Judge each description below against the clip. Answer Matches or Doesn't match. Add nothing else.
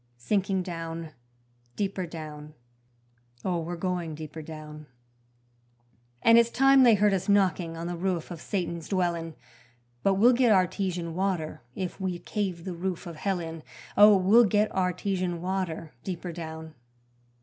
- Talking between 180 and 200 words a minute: Doesn't match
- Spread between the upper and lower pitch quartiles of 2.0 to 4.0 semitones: Matches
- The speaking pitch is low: Doesn't match